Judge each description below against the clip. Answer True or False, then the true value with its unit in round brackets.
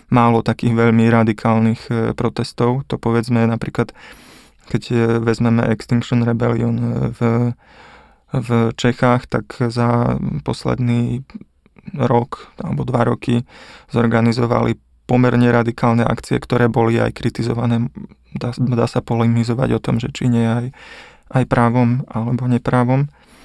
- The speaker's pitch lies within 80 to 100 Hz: False (120 Hz)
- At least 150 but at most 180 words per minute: False (115 wpm)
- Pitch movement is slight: True (1.0 semitones)